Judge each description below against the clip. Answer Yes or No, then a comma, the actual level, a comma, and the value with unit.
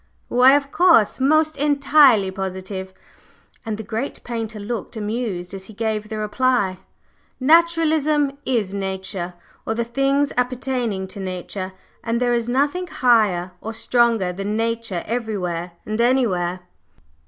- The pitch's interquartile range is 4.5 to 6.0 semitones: Yes, average, 5.2 semitones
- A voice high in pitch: Yes, high, 225 Hz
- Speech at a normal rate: No, slow, 130 wpm